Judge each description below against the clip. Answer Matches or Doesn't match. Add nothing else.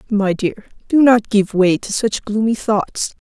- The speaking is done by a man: Doesn't match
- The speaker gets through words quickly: Doesn't match